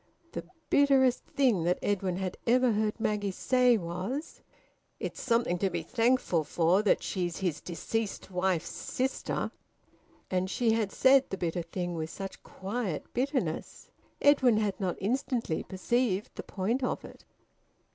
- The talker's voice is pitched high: Yes, high, 205 Hz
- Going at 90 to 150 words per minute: Yes, average, 145 wpm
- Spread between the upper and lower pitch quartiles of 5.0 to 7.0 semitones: Yes, wide, 5.4 semitones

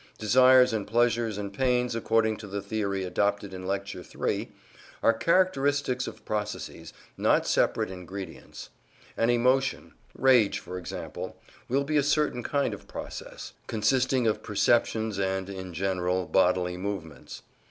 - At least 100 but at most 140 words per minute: Yes, slow, 135 wpm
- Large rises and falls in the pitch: No, average, 4.7 semitones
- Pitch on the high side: No, low, 110 Hz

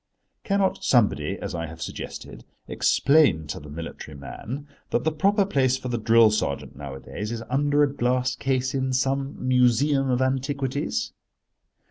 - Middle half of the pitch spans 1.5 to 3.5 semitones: No, average, 4.6 semitones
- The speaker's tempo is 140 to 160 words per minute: Yes, average, 150 wpm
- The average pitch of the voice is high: No, low, 130 Hz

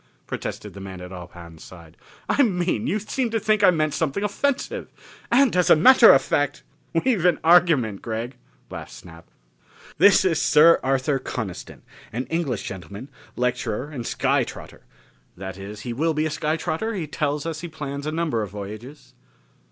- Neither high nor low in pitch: Yes, medium, 145 Hz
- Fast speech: No, average, 180 wpm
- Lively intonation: Yes, wide, 7.7 semitones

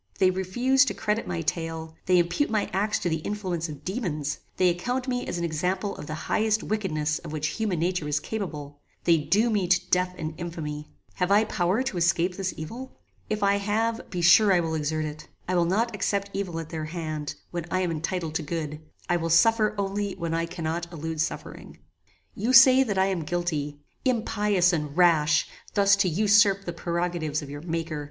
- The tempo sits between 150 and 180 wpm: No, average, 200 wpm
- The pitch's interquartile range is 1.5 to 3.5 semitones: No, average, 4.0 semitones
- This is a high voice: No, medium, 175 Hz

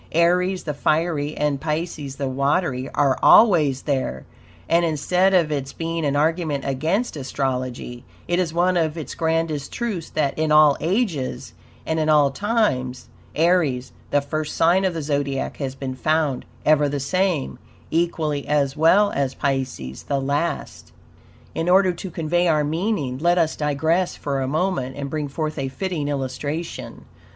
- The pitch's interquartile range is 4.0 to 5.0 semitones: No, average, 3.6 semitones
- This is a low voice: No, medium, 150 Hz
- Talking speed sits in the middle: Yes, average, 160 wpm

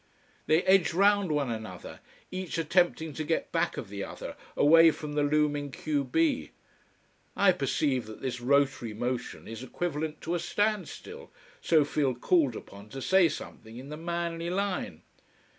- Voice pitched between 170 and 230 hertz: No, medium, 150 Hz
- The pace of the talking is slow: No, average, 160 wpm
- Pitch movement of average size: Yes, average, 4.9 semitones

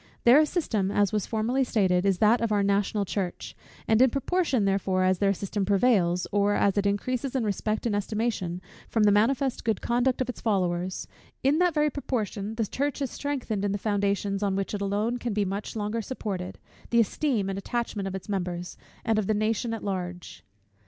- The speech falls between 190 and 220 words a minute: Yes, average, 200 wpm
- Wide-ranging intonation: No, average, 3.3 semitones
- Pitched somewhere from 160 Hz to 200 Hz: No, high, 210 Hz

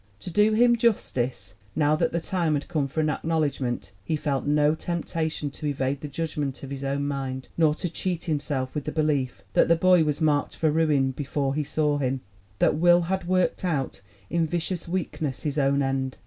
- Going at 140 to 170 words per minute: No, average, 200 wpm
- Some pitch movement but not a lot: Yes, average, 3.2 semitones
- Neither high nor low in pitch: Yes, medium, 150 Hz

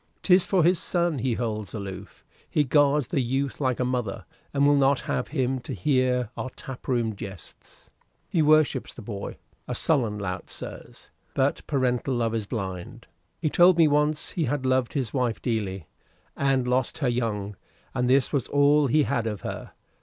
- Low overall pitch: Yes, low, 130 Hz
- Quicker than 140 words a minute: Yes, average, 180 wpm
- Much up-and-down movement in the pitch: No, average, 4.2 semitones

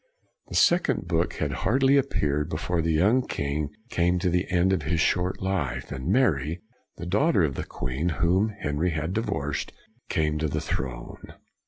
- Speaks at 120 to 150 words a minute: No, average, 170 wpm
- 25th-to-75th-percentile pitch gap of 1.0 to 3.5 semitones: No, average, 4.2 semitones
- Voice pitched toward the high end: No, very low, 85 Hz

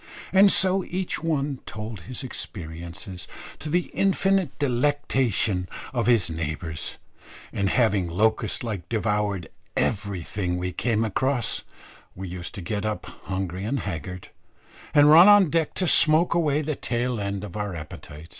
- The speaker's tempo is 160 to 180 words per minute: No, average, 145 wpm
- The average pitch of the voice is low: Yes, low, 110 Hz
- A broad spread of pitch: Yes, wide, 7.8 semitones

